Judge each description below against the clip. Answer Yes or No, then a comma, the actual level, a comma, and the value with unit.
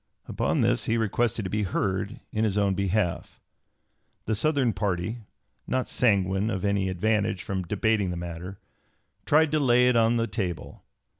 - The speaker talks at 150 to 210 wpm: Yes, average, 160 wpm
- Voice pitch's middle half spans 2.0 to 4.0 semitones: Yes, average, 3.3 semitones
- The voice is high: No, low, 105 Hz